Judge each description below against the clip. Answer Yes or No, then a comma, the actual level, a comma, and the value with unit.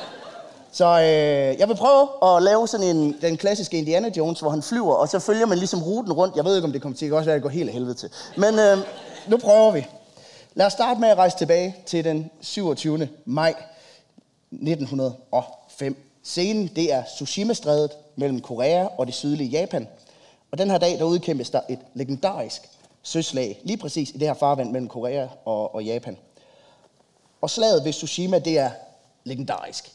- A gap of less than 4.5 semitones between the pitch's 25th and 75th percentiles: No, average, 5.1 semitones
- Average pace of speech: Yes, average, 185 wpm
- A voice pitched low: No, medium, 160 Hz